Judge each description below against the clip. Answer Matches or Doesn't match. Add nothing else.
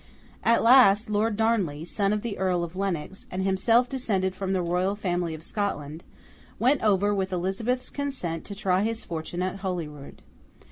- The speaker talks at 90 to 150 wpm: Doesn't match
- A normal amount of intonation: Matches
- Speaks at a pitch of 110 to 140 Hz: Doesn't match